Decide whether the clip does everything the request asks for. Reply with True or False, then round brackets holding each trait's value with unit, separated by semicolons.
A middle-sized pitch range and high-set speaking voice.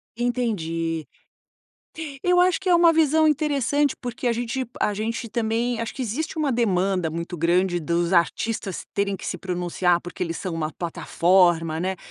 False (6.2 semitones; 200 Hz)